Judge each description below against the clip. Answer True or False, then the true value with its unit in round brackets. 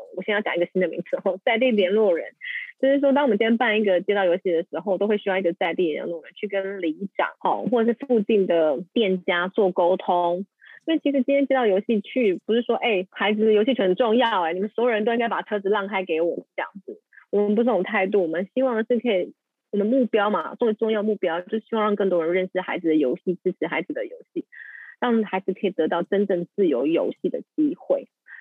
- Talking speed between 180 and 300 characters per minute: False (355 characters per minute)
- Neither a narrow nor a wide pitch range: True (4.5 semitones)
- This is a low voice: False (205 Hz)